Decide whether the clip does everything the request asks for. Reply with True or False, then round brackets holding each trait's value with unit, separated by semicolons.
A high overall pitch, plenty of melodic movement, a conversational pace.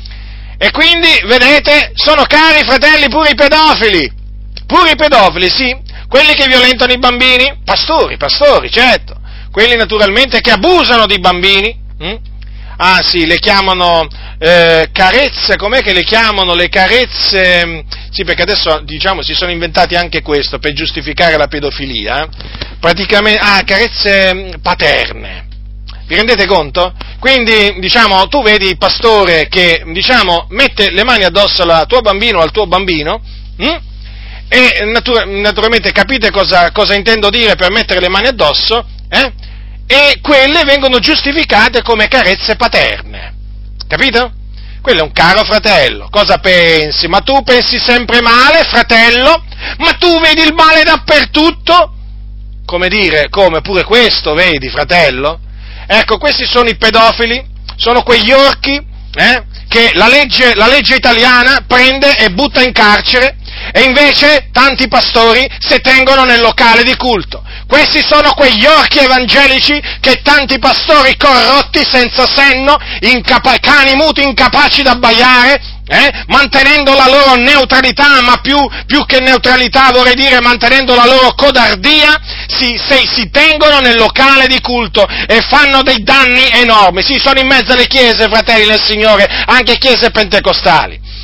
True (235 Hz; 6.4 semitones; 140 wpm)